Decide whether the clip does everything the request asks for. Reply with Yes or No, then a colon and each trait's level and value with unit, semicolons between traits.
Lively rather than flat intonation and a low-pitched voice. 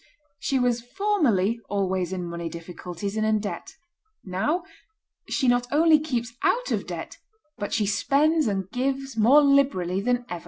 No: wide, 6.5 semitones; high, 235 Hz